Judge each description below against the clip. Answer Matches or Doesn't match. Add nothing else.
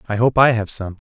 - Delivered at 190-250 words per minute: Doesn't match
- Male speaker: Matches